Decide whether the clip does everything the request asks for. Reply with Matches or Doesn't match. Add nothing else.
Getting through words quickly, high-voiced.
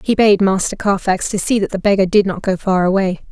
Matches